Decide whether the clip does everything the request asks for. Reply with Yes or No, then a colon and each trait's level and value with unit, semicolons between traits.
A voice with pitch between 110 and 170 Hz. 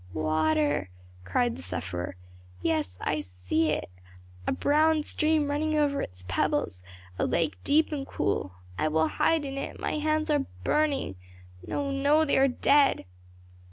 No: very high, 270 Hz